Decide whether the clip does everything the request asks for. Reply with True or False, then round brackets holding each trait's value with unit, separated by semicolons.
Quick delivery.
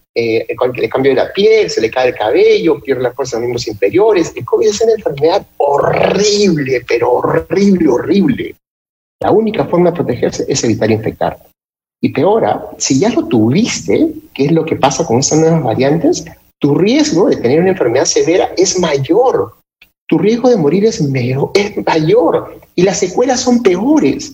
False (175 wpm)